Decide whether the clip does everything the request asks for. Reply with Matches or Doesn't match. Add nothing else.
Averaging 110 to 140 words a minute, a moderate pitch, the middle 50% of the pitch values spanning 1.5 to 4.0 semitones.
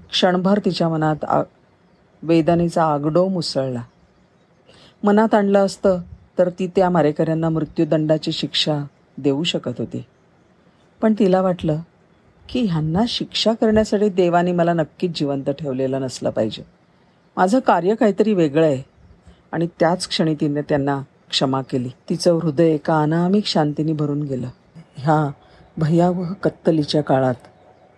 Matches